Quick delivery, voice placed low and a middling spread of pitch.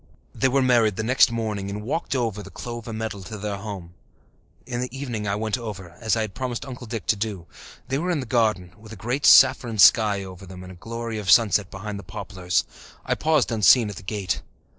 Yes: fast, 225 wpm; low, 110 Hz; average, 3.3 semitones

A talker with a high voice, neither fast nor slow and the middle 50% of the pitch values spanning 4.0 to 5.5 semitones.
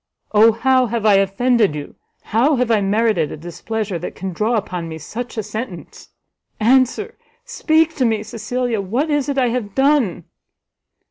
Yes: high, 225 Hz; average, 170 wpm; average, 4.4 semitones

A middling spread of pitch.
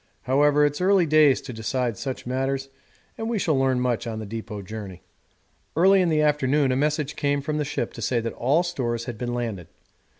Yes: average, 4.1 semitones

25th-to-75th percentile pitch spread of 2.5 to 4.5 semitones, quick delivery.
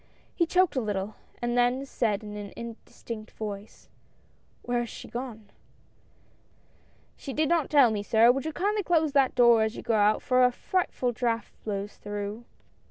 No: average, 4.1 semitones; average, 180 wpm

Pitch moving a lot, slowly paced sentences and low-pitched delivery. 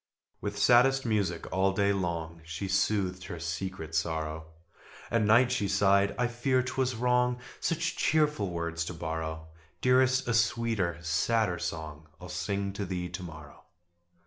No: wide, 5.9 semitones; average, 145 wpm; very low, 95 Hz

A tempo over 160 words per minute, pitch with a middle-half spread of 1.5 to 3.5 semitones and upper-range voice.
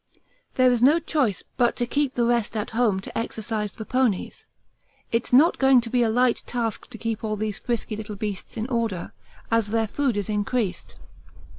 Yes: average, 190 wpm; narrow, 2.6 semitones; high, 230 Hz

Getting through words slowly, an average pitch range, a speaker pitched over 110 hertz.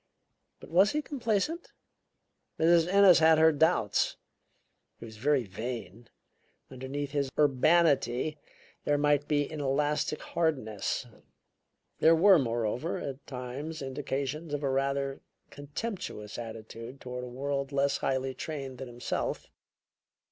Yes: slow, 120 wpm; average, 3.8 semitones; medium, 140 Hz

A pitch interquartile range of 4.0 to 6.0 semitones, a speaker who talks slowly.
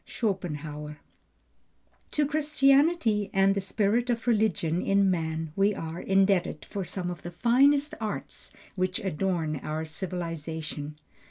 Yes: average, 5.3 semitones; slow, 120 wpm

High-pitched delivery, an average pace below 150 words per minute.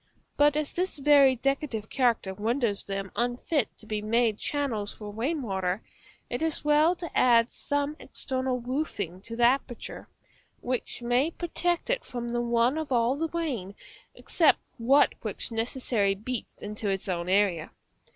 No: high, 245 Hz; average, 155 wpm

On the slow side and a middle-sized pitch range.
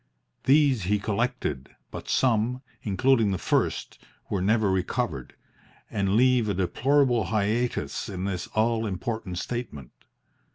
Yes: slow, 120 wpm; average, 4.2 semitones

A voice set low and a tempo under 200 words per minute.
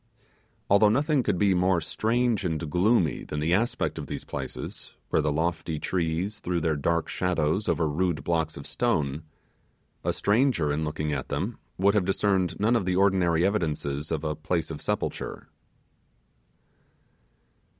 Yes: very low, 85 Hz; average, 150 wpm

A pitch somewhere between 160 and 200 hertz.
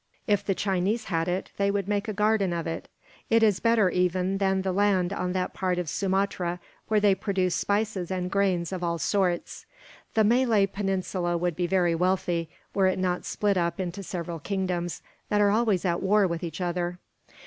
Yes: high, 190 Hz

